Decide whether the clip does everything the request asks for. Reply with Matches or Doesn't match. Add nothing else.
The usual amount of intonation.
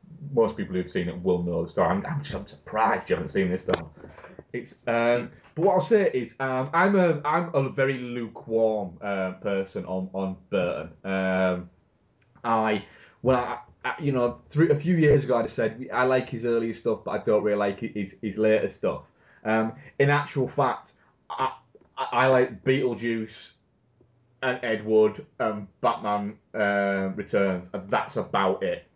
Matches